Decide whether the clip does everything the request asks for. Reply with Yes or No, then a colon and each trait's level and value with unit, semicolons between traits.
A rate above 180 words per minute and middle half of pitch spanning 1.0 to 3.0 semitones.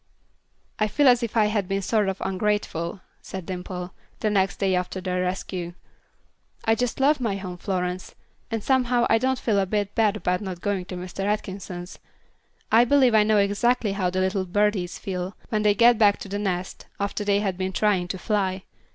Yes: average, 195 wpm; narrow, 2.6 semitones